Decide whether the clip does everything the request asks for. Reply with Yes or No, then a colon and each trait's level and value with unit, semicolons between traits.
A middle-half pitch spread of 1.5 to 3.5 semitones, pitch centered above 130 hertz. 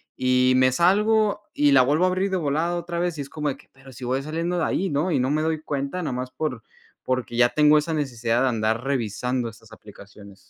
No: average, 4.6 semitones; medium, 140 Hz